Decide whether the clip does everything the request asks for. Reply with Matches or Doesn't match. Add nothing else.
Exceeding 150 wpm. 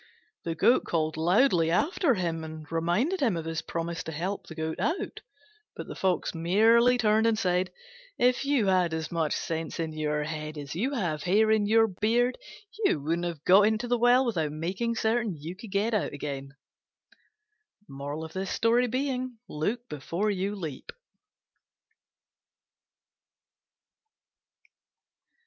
Doesn't match